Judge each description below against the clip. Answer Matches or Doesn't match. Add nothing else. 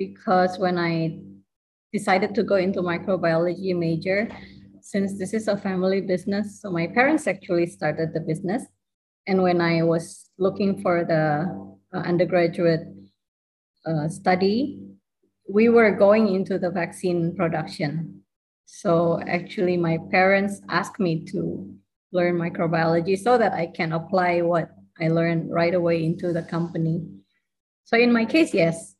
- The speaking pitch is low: Doesn't match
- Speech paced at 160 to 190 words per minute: Doesn't match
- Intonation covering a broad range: Doesn't match